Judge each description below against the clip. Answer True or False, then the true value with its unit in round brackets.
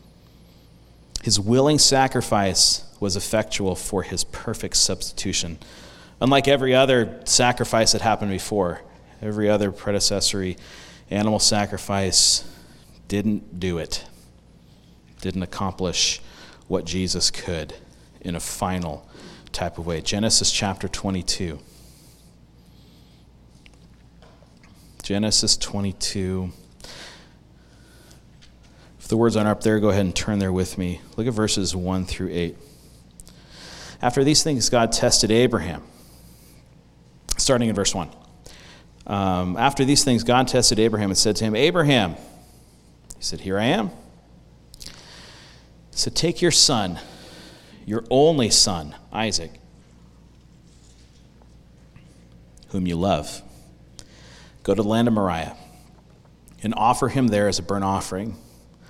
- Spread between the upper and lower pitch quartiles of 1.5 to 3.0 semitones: False (5.4 semitones)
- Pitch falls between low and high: False (100 Hz)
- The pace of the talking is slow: True (115 wpm)